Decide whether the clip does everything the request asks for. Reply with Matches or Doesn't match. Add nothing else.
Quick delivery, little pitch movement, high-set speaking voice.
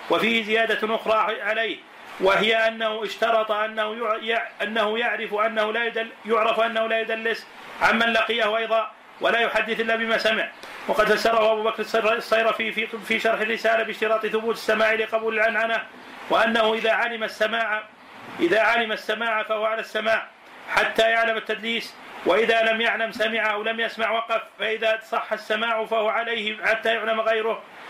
Matches